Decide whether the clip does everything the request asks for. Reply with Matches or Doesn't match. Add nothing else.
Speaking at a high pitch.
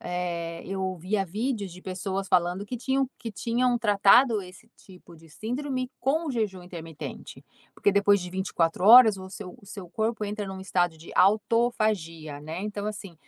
Matches